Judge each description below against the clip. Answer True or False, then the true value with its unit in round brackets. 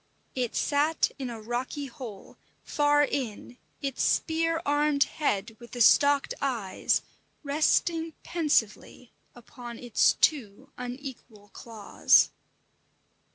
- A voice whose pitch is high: True (265 Hz)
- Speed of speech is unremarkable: False (105 wpm)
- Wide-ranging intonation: False (3.7 semitones)